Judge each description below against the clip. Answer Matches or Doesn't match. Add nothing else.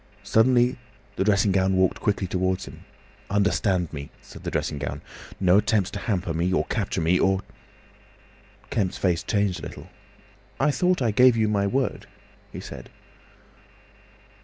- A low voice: Matches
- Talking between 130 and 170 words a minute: Matches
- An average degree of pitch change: Matches